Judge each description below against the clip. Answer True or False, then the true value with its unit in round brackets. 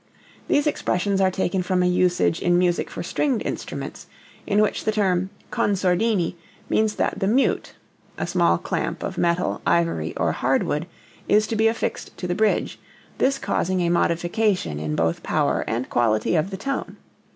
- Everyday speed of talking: True (170 wpm)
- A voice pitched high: False (180 Hz)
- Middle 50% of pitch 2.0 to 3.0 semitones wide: False (3.7 semitones)